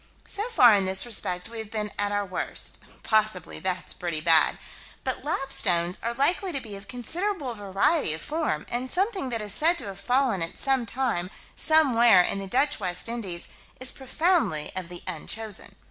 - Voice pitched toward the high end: Yes, high, 225 Hz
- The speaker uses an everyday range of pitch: No, wide, 6.2 semitones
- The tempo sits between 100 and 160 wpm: No, average, 175 wpm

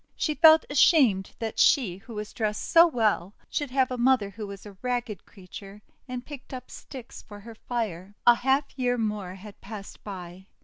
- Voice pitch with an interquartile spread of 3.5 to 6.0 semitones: Yes, average, 4.2 semitones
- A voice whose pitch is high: Yes, high, 220 Hz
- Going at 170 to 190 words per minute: Yes, average, 185 wpm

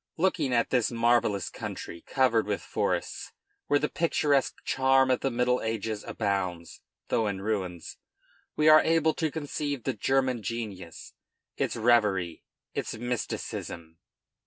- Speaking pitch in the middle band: No, low, 120 Hz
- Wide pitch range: No, average, 4.8 semitones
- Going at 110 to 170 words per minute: Yes, slow, 135 wpm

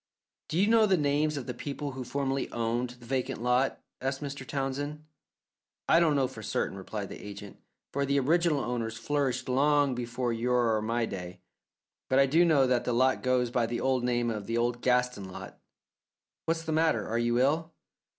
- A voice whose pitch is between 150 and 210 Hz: No, low, 130 Hz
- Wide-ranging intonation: No, average, 3.3 semitones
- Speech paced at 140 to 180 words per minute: No, average, 190 wpm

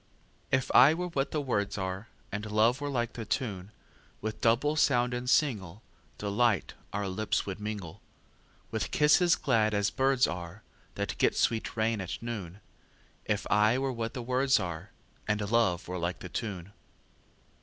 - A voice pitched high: No, low, 110 Hz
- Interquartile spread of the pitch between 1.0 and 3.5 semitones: No, average, 4.0 semitones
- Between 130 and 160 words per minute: Yes, average, 140 wpm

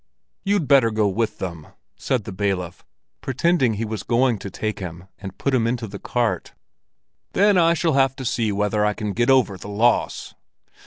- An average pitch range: Yes, average, 4.6 semitones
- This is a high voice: No, low, 110 Hz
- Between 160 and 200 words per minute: Yes, average, 190 wpm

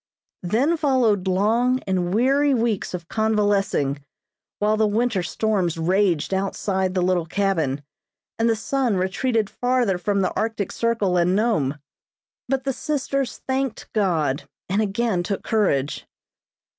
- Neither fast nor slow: No, slow, 130 wpm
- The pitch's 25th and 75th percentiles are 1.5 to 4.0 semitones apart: No, average, 4.4 semitones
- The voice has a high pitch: Yes, high, 205 Hz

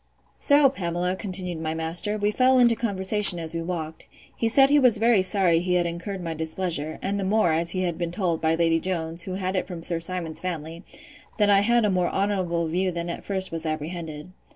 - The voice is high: No, medium, 180 Hz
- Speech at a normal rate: No, fast, 220 wpm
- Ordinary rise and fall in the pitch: Yes, average, 3.2 semitones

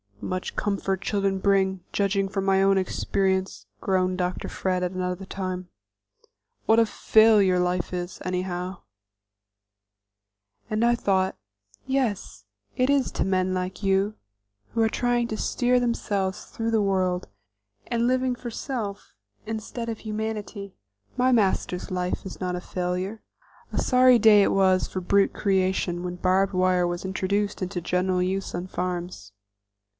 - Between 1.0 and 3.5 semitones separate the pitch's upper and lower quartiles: Yes, average, 2.8 semitones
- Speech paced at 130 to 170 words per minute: Yes, average, 145 wpm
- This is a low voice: No, high, 190 Hz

